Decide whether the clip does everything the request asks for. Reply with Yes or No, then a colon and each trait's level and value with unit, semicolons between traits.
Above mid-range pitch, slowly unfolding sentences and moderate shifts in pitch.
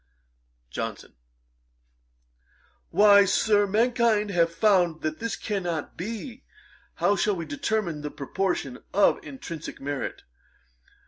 Yes: high, 200 Hz; slow, 105 wpm; average, 4.6 semitones